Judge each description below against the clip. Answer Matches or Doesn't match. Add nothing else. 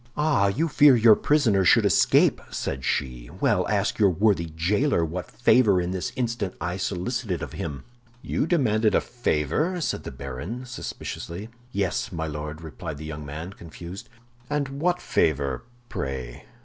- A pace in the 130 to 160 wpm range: Matches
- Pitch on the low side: Matches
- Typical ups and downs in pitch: Doesn't match